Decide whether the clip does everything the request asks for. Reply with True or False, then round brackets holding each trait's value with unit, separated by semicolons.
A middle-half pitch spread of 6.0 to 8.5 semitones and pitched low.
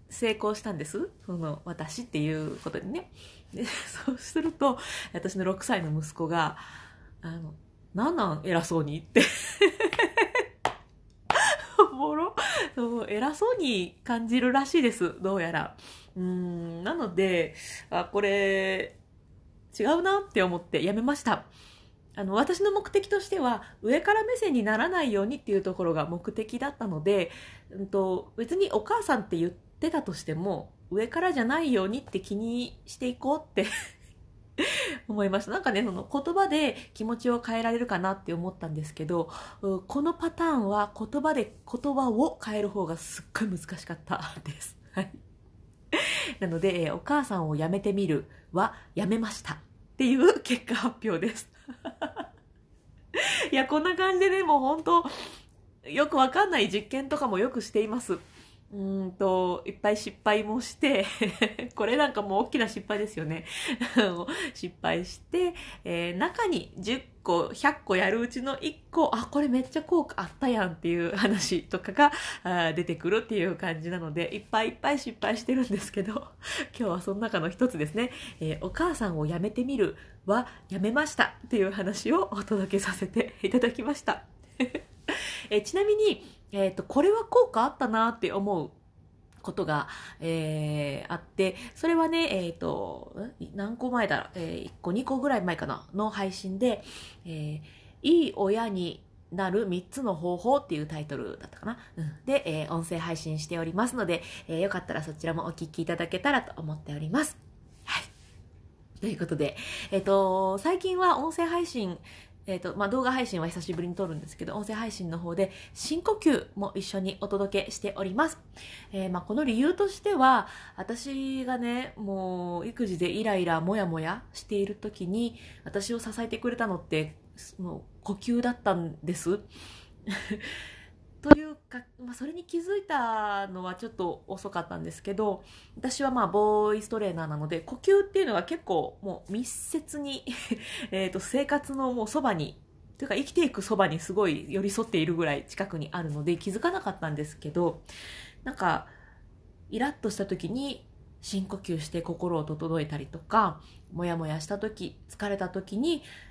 False (6.9 semitones; 205 Hz)